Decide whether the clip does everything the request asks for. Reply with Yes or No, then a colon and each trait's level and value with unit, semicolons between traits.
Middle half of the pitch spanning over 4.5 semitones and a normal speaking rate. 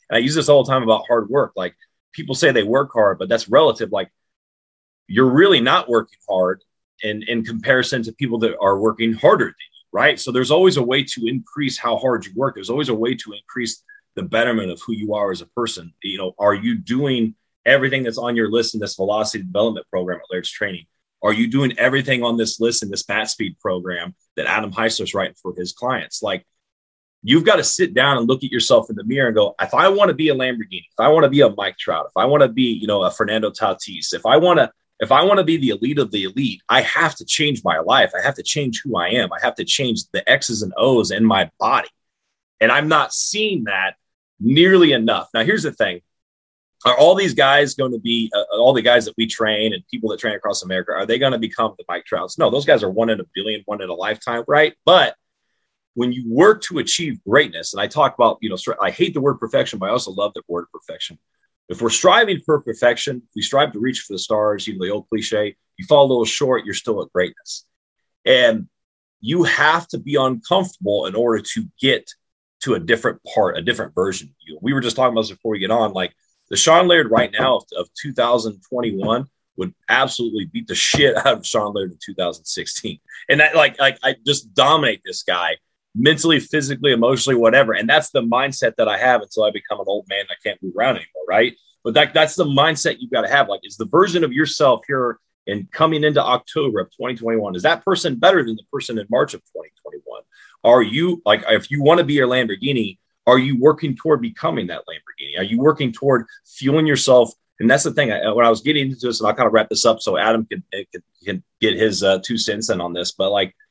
No: average, 5.1 semitones; fast, 240 wpm